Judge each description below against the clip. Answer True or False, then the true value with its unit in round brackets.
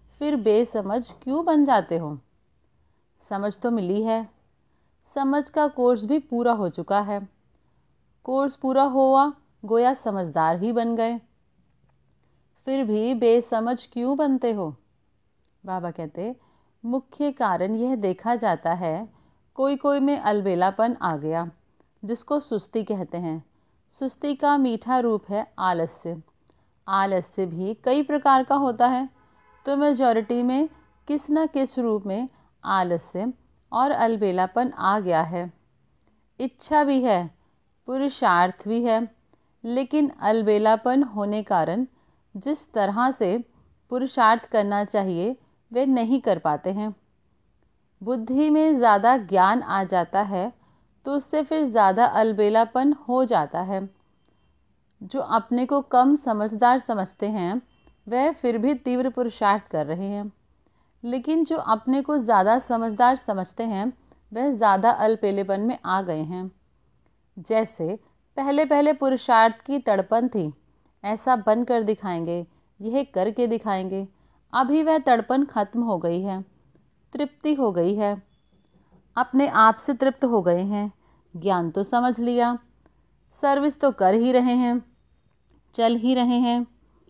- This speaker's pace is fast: False (130 wpm)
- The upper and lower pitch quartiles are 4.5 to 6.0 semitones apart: True (5.0 semitones)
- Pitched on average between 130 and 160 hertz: False (230 Hz)